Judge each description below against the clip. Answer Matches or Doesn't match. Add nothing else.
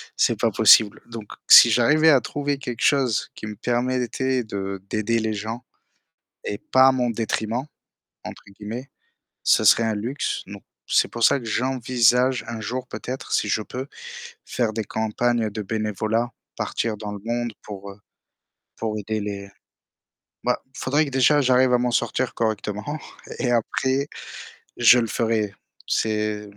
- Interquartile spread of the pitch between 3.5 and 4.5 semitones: Doesn't match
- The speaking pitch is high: Doesn't match